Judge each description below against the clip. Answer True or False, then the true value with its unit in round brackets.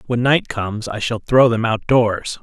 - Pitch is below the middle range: True (115 Hz)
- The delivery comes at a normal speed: False (225 wpm)